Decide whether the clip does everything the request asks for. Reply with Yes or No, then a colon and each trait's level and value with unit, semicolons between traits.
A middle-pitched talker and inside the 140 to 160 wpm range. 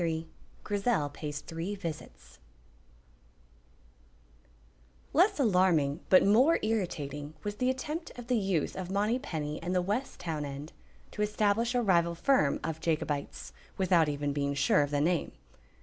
Yes: medium, 175 Hz; average, 145 wpm